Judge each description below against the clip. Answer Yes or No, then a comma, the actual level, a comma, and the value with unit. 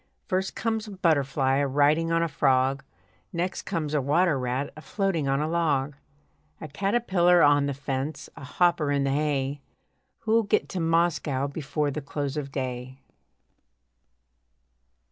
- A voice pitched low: No, medium, 150 Hz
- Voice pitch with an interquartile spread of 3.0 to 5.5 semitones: Yes, average, 3.8 semitones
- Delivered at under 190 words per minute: Yes, average, 150 wpm